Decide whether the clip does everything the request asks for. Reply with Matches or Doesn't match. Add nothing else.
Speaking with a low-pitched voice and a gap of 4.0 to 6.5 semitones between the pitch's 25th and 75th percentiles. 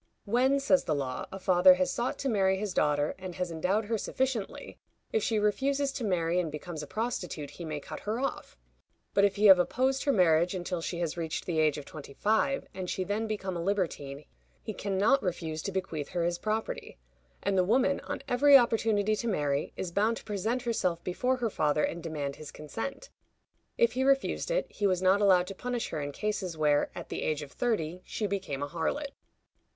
Doesn't match